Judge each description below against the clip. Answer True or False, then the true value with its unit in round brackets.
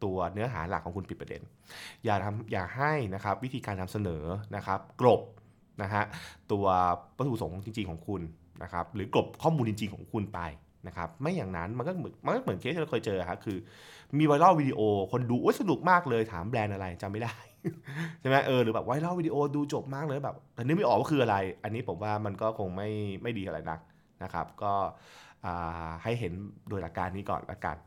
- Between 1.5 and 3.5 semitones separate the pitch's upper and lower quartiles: False (4.9 semitones)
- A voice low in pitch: True (105 Hz)